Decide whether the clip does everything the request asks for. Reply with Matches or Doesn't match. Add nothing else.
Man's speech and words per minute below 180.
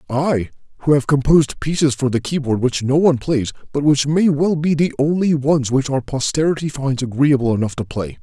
Doesn't match